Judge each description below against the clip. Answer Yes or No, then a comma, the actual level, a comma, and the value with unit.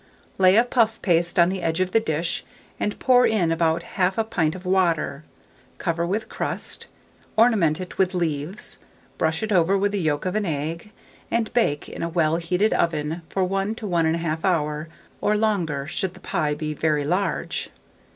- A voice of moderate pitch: Yes, medium, 175 Hz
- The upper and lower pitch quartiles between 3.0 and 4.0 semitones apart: Yes, average, 3.7 semitones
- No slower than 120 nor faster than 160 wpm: No, average, 180 wpm